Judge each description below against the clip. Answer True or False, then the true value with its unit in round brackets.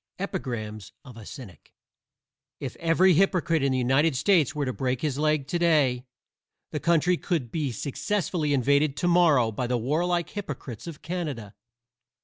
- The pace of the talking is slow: False (155 wpm)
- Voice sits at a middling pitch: True (145 Hz)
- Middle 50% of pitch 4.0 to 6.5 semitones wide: True (5.1 semitones)